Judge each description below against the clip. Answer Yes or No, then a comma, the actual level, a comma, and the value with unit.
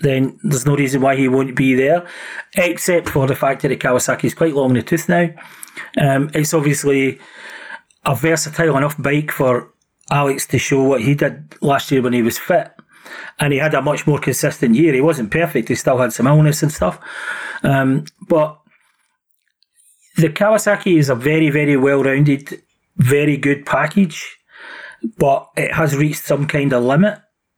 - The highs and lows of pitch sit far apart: No, average, 3.2 semitones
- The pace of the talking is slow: No, average, 180 wpm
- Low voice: No, medium, 145 Hz